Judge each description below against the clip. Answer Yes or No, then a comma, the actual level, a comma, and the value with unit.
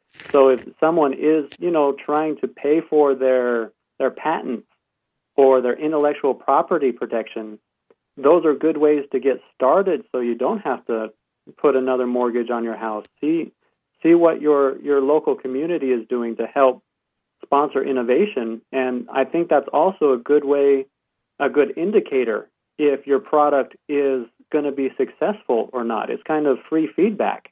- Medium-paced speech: Yes, average, 165 wpm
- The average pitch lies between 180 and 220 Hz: No, medium, 140 Hz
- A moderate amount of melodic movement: Yes, average, 3.2 semitones